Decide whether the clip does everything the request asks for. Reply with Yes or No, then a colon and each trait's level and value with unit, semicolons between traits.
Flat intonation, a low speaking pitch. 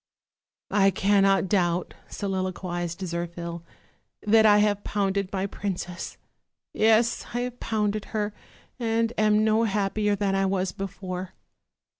No: narrow, 2.3 semitones; high, 200 Hz